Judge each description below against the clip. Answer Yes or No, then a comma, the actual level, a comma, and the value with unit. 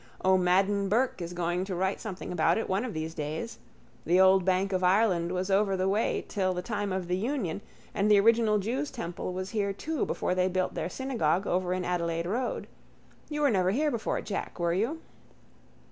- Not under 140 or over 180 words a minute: No, average, 200 wpm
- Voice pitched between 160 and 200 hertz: Yes, high, 190 Hz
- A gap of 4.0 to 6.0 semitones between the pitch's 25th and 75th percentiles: No, average, 3.0 semitones